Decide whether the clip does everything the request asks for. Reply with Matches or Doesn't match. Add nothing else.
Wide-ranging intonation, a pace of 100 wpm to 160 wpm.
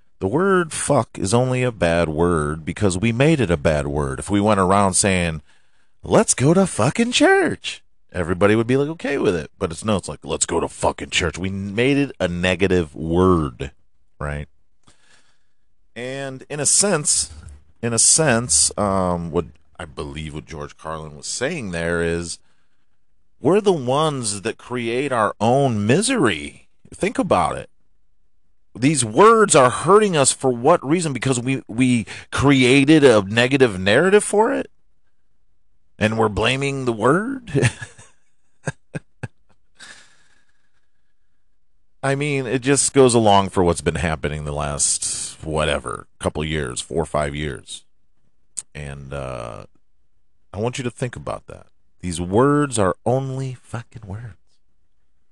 Matches